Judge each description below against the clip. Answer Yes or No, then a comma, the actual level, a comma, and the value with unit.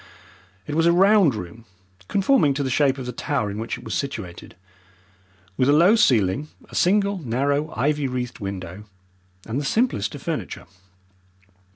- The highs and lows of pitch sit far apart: Yes, wide, 6.5 semitones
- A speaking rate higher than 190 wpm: No, average, 165 wpm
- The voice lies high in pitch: No, medium, 140 Hz